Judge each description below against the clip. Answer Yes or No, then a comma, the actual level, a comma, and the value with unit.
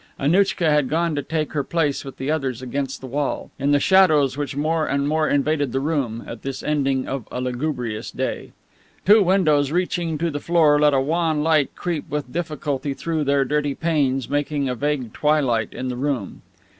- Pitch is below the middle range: No, medium, 145 Hz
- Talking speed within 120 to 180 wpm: No, average, 195 wpm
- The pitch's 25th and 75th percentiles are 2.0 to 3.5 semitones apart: Yes, average, 2.7 semitones